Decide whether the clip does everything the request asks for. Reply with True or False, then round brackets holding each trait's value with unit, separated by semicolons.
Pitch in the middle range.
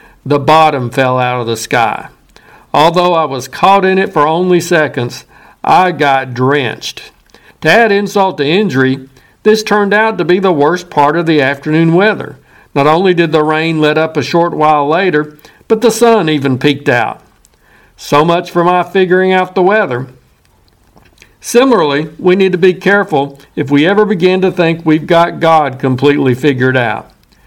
True (155 Hz)